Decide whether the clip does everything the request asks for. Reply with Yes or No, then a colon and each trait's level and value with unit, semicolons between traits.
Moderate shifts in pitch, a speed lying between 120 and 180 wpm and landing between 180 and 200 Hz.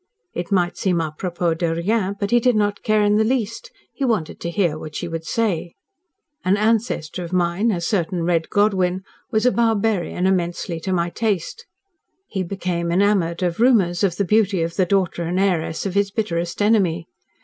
No: average, 3.6 semitones; average, 190 wpm; medium, 185 Hz